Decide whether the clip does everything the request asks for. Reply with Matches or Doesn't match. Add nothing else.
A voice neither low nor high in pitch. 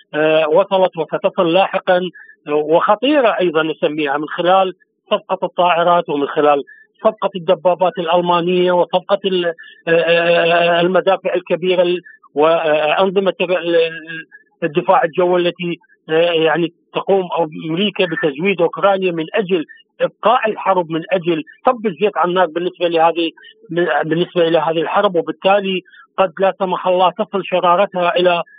Matches